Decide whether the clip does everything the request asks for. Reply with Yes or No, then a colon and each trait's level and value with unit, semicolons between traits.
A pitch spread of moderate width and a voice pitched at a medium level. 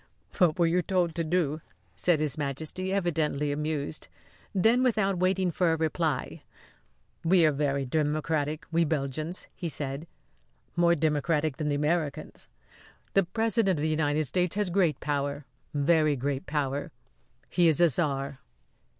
Yes: average, 3.2 semitones; medium, 155 Hz